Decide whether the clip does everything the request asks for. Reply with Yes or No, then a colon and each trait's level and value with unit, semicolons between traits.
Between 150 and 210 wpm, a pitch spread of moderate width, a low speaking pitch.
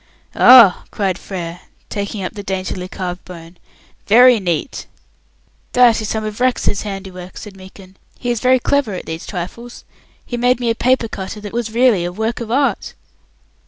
No: average, 170 wpm; average, 4.4 semitones; high, 210 Hz